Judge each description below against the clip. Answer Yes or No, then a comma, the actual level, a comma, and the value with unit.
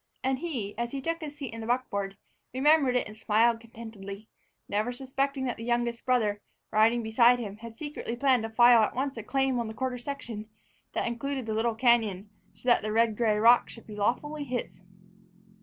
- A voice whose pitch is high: Yes, high, 235 Hz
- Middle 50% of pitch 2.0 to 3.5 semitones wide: Yes, average, 2.9 semitones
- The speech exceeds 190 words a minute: Yes, average, 200 wpm